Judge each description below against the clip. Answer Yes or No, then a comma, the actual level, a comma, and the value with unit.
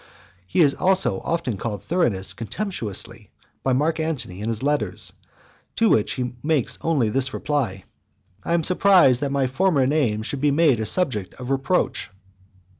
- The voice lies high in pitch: No, low, 135 Hz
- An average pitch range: No, wide, 6.3 semitones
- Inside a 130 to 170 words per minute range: Yes, average, 160 wpm